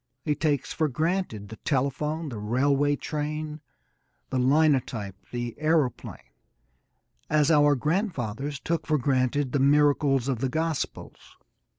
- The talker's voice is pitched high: No, medium, 145 Hz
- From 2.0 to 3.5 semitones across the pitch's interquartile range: Yes, average, 3.2 semitones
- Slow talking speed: Yes, slow, 120 wpm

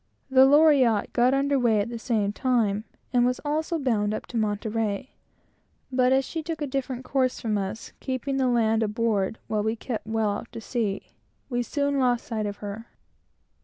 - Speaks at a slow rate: No, average, 185 wpm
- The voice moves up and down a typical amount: Yes, average, 3.5 semitones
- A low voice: No, high, 235 Hz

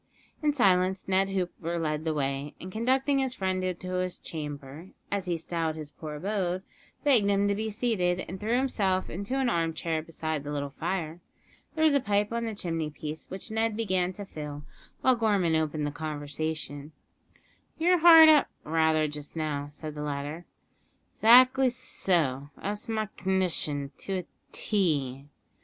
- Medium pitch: Yes, medium, 180 Hz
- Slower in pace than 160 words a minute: No, average, 165 wpm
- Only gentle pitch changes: No, wide, 5.4 semitones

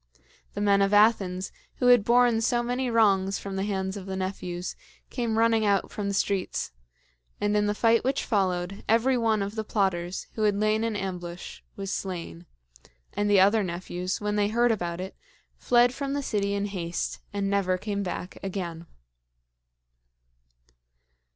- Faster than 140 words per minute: Yes, average, 170 wpm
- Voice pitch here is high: Yes, high, 200 Hz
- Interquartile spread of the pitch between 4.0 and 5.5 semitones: No, average, 2.9 semitones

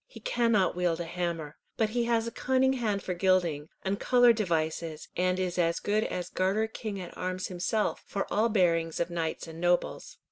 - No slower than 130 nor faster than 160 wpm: No, average, 190 wpm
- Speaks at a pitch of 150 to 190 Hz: Yes, medium, 185 Hz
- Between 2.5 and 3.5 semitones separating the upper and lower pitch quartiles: No, average, 4.4 semitones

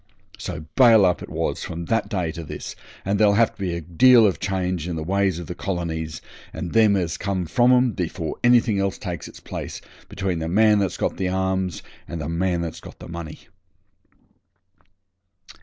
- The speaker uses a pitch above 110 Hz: No, very low, 95 Hz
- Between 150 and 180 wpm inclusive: No, average, 195 wpm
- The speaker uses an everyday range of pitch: Yes, average, 3.1 semitones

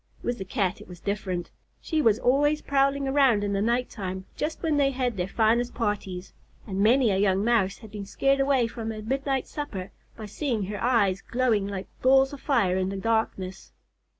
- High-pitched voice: Yes, high, 225 Hz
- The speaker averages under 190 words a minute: No, average, 200 wpm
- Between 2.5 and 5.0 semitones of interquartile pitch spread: No, wide, 5.4 semitones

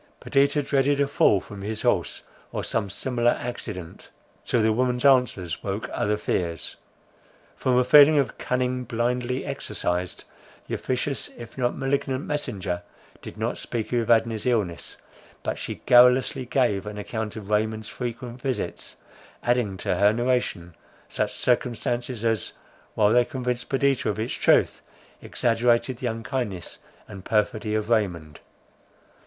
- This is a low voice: Yes, low, 120 Hz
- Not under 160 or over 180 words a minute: No, slow, 135 wpm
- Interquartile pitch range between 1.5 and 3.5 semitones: Yes, average, 3.2 semitones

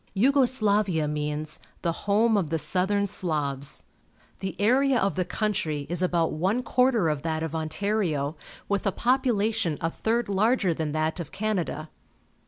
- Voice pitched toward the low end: No, medium, 185 Hz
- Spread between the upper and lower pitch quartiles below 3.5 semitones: No, wide, 5.5 semitones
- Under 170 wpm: Yes, average, 160 wpm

